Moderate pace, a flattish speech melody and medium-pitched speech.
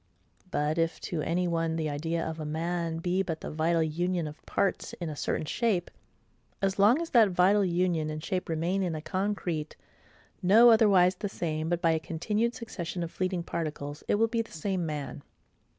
No: average, 195 wpm; average, 3.2 semitones; medium, 170 Hz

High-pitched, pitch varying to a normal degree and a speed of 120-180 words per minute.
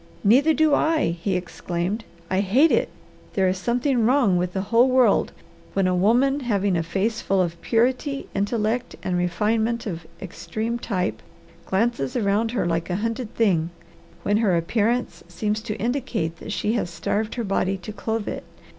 Yes: high, 210 Hz; average, 4.4 semitones; average, 170 wpm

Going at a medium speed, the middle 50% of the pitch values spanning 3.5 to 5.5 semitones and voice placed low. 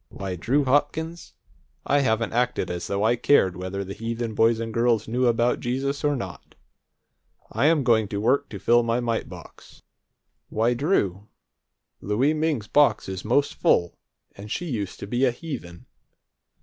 Yes: average, 160 wpm; average, 4.9 semitones; low, 115 Hz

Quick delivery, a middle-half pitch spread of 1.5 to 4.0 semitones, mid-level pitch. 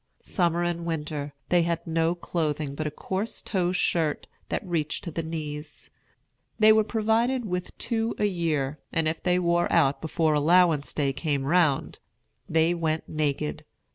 No: average, 160 wpm; average, 2.9 semitones; medium, 165 Hz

